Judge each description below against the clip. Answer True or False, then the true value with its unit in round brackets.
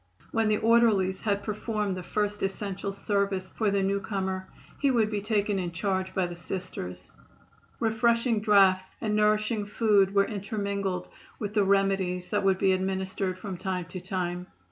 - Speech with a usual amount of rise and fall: False (2.1 semitones)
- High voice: True (200 Hz)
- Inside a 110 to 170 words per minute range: True (160 wpm)